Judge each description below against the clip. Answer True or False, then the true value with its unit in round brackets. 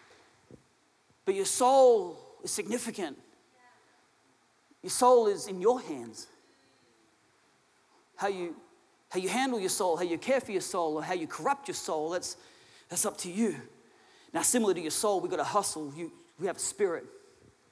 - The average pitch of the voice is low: False (240 Hz)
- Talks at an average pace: True (160 wpm)